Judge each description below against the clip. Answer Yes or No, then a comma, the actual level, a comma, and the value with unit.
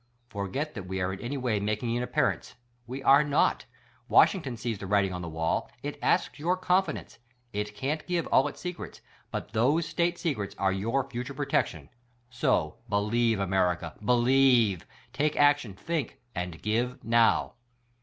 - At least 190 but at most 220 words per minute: No, average, 165 wpm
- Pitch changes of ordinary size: No, wide, 6.1 semitones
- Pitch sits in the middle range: No, low, 120 Hz